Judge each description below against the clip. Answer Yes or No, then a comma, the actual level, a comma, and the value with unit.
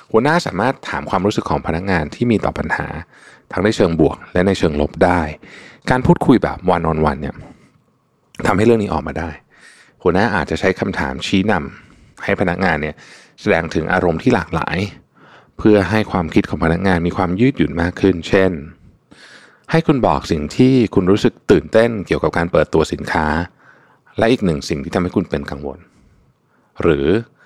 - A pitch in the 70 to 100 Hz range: Yes, very low, 90 Hz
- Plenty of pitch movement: No, average, 4.0 semitones